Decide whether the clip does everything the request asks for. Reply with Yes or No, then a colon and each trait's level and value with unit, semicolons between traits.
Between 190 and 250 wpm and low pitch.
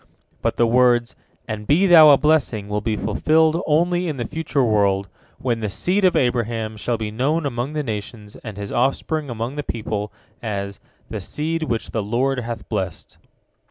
No: average, 180 wpm; low, 120 Hz